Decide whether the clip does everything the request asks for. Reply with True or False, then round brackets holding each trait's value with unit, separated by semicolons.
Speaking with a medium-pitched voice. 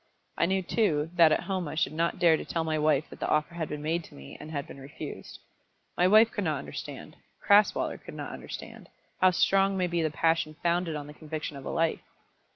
True (165 Hz)